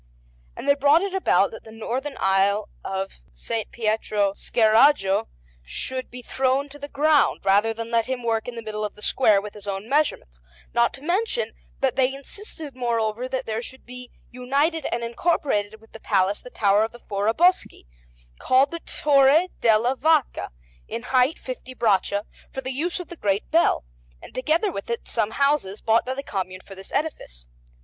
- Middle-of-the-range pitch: No, high, 245 Hz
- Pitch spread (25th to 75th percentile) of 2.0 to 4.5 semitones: No, average, 4.9 semitones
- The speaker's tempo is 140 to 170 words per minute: No, average, 185 wpm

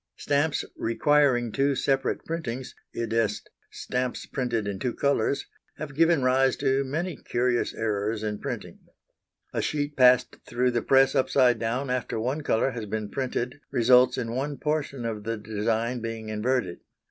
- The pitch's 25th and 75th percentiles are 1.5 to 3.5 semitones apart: Yes, average, 3.2 semitones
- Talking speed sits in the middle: Yes, average, 150 wpm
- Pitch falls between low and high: No, low, 125 Hz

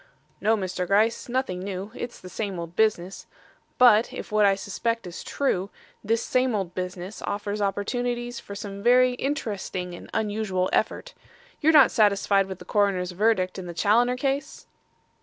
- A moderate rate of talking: Yes, average, 160 wpm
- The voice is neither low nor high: No, high, 205 Hz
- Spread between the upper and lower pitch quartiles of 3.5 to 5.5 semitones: Yes, average, 4.2 semitones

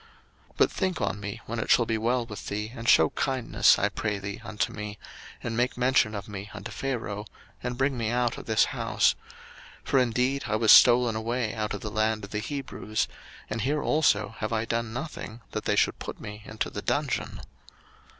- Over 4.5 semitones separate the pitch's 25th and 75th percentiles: No, average, 2.7 semitones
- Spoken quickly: Yes, fast, 210 wpm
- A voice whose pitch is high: No, low, 110 Hz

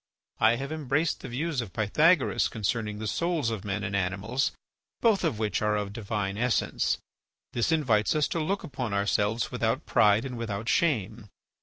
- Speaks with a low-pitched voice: Yes, low, 115 Hz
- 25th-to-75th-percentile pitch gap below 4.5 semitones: No, wide, 5.5 semitones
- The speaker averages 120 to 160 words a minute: No, average, 170 wpm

